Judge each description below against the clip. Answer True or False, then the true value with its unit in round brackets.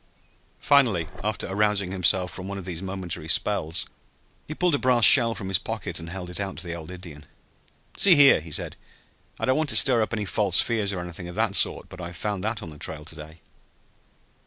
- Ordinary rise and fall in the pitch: True (4.1 semitones)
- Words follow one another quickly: True (220 wpm)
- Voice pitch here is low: True (95 Hz)